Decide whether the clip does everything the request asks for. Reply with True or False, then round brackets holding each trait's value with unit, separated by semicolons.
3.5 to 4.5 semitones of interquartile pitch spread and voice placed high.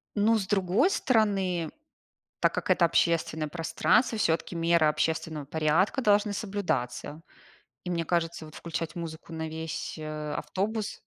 False (4.2 semitones; 170 Hz)